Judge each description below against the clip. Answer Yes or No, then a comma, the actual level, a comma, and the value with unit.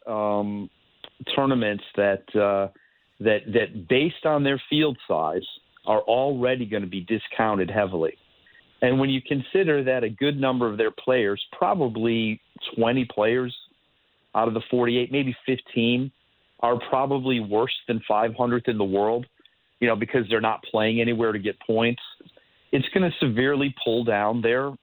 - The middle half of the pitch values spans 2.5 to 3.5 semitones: Yes, average, 3.2 semitones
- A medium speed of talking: Yes, average, 150 wpm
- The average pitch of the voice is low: Yes, low, 120 Hz